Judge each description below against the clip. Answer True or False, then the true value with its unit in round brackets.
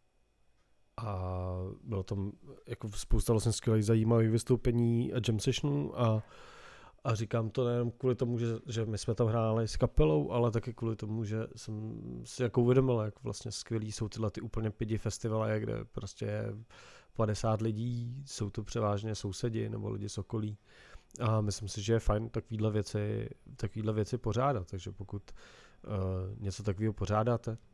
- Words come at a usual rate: True (160 wpm)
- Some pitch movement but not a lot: False (2.1 semitones)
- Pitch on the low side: True (110 Hz)